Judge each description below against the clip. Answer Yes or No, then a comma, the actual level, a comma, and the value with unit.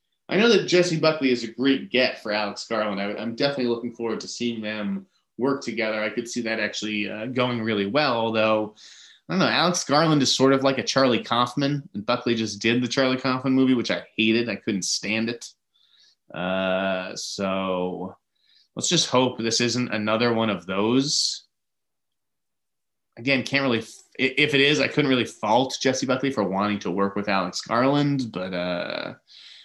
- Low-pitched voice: Yes, low, 115 Hz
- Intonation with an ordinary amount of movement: Yes, average, 4.1 semitones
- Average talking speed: Yes, average, 185 wpm